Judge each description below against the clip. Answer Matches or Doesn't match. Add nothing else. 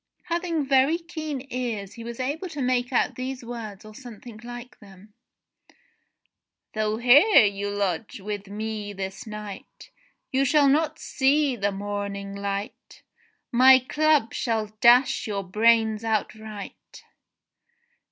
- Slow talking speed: Matches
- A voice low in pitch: Doesn't match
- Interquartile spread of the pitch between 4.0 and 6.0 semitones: Matches